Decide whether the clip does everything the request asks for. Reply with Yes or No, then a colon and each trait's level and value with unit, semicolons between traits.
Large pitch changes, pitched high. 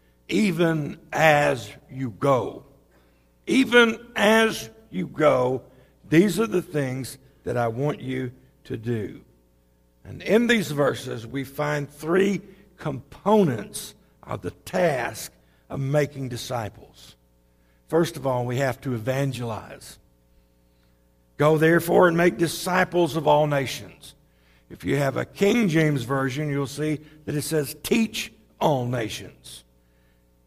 No: wide, 7.1 semitones; medium, 140 Hz